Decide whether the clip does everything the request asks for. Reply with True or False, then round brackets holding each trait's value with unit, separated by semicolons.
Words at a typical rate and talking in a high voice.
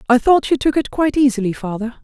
False (235 wpm; 255 Hz)